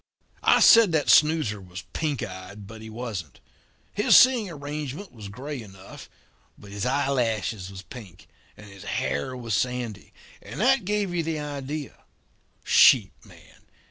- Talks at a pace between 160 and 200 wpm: No, average, 150 wpm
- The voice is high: No, low, 125 Hz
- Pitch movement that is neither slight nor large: No, wide, 7.0 semitones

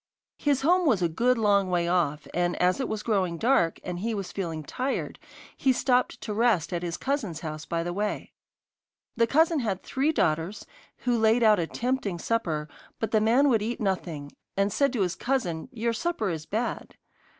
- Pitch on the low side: No, high, 210 Hz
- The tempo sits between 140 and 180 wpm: No, average, 195 wpm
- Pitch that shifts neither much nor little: No, wide, 6.0 semitones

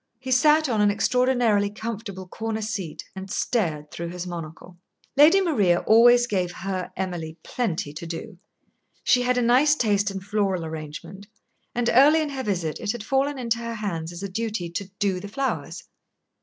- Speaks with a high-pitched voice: Yes, high, 205 Hz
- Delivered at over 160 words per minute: Yes, average, 175 wpm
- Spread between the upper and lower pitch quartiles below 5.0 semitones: No, average, 5.3 semitones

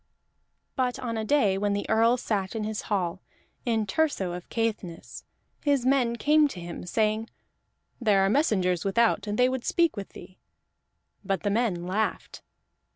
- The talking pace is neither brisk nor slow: Yes, average, 160 wpm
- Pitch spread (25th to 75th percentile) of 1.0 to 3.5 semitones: No, average, 4.1 semitones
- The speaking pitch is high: Yes, high, 215 Hz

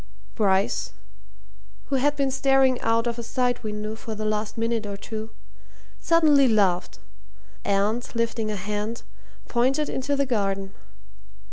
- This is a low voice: No, high, 230 Hz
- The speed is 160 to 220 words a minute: No, slow, 135 wpm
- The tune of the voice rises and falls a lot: No, average, 3.6 semitones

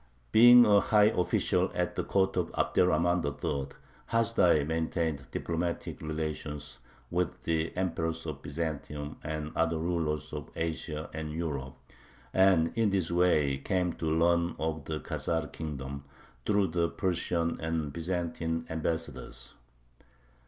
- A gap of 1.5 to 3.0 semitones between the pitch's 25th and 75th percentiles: Yes, narrow, 2.4 semitones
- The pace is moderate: No, slow, 125 wpm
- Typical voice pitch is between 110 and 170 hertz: No, very low, 80 Hz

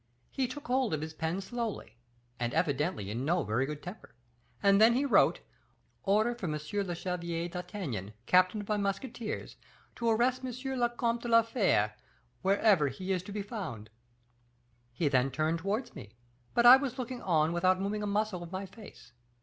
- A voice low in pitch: No, high, 195 Hz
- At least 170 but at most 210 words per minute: Yes, average, 180 wpm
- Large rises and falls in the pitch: Yes, wide, 6.4 semitones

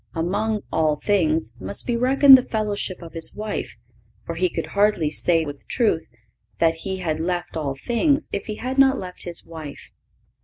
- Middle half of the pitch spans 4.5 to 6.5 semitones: Yes, average, 5.1 semitones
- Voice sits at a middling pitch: Yes, medium, 180 Hz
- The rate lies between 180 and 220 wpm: Yes, average, 185 wpm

